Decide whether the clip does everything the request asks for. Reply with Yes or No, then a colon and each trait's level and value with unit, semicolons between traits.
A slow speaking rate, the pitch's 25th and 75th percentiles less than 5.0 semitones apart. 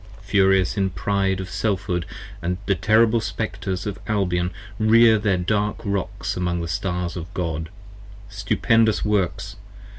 Yes: slow, 130 wpm; average, 2.8 semitones